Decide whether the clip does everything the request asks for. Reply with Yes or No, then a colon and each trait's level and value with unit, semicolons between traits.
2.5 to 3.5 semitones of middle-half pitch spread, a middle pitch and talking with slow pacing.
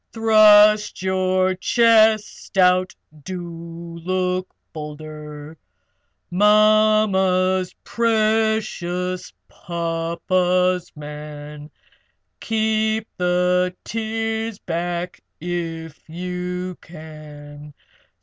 No: average, 4.2 semitones; medium, 180 Hz; slow, 60 wpm